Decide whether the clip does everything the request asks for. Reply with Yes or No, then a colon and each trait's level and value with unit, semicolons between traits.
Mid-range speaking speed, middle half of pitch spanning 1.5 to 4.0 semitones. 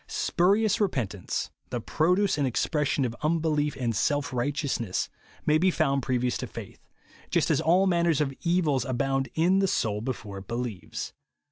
No: average, 165 wpm; wide, 5.5 semitones